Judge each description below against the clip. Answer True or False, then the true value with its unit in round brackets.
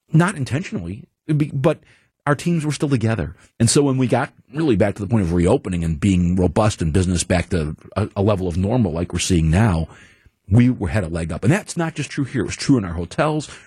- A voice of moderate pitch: False (110 Hz)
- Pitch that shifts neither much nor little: False (7.6 semitones)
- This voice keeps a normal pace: False (235 wpm)